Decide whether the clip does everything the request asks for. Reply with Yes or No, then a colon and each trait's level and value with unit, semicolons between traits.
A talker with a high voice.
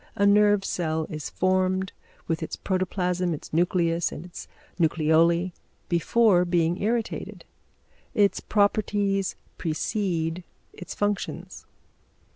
No: medium, 180 Hz